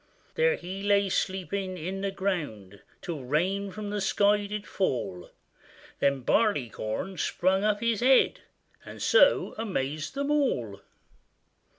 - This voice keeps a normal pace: No, slow, 125 wpm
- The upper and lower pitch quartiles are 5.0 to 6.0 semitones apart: Yes, wide, 5.5 semitones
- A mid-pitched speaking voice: No, high, 195 Hz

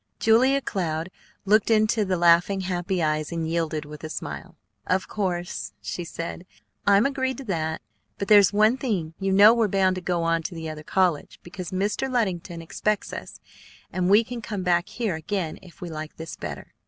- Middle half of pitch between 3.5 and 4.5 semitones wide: Yes, average, 4.0 semitones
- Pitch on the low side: No, medium, 185 Hz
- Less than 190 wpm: No, average, 195 wpm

